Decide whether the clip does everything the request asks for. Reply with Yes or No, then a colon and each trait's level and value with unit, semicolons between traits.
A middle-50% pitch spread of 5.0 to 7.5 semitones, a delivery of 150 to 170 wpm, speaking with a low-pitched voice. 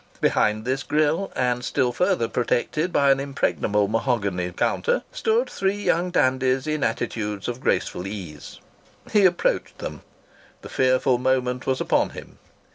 No: average, 5.3 semitones; average, 140 wpm; low, 130 Hz